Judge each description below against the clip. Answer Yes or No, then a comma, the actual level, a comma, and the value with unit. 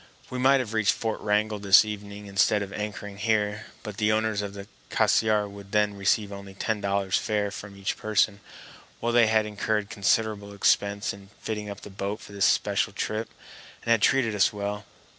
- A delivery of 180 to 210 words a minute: Yes, average, 190 wpm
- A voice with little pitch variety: Yes, narrow, 1.3 semitones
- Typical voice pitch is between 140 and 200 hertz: No, low, 105 Hz